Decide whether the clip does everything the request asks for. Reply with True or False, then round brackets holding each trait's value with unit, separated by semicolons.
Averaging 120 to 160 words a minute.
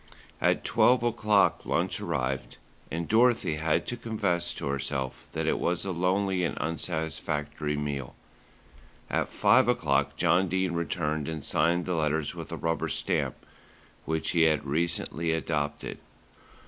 True (140 wpm)